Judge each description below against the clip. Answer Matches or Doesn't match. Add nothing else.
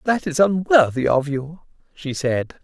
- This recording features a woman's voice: Doesn't match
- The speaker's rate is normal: Matches